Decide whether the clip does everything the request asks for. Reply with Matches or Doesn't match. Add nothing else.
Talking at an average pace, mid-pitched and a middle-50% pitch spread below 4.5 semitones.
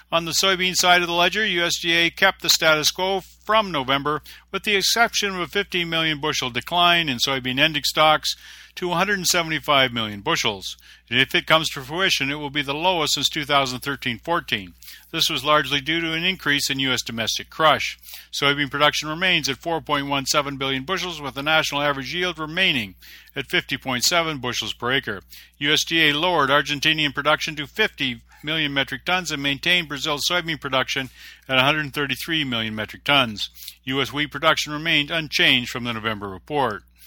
Matches